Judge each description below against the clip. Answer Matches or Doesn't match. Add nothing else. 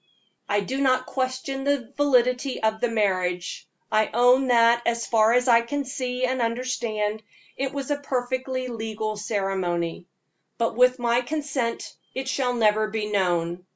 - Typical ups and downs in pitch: Matches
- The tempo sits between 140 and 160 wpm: Matches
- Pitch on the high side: Matches